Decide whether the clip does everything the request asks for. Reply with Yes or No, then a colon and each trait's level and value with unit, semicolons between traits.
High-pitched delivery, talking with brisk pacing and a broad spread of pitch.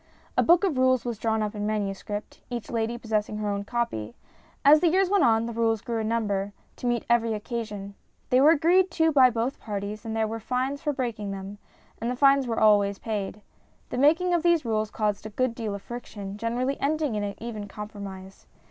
No: high, 225 Hz; fast, 210 wpm; average, 3.7 semitones